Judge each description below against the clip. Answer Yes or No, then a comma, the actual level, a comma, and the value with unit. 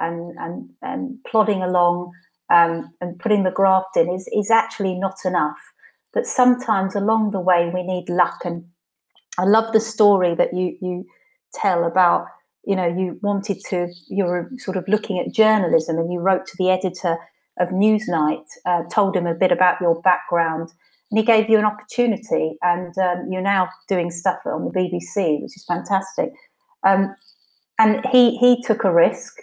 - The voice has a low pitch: No, medium, 185 Hz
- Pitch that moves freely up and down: No, average, 3.4 semitones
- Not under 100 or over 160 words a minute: No, average, 175 wpm